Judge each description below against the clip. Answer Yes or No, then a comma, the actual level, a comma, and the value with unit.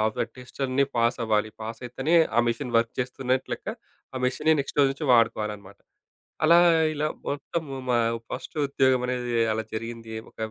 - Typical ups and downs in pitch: Yes, average, 3.0 semitones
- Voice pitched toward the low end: Yes, low, 125 Hz